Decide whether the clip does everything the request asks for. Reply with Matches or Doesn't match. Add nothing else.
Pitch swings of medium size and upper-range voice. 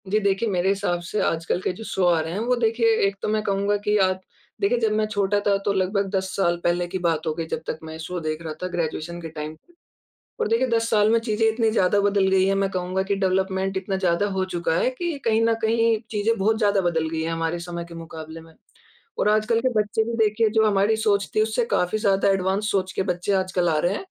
Matches